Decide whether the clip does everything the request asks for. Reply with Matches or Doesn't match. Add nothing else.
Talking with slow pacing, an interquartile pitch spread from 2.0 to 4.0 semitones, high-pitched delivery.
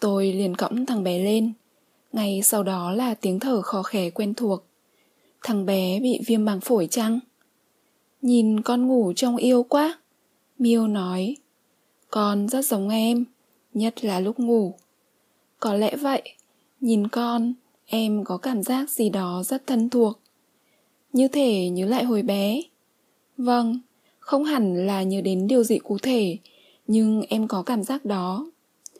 Matches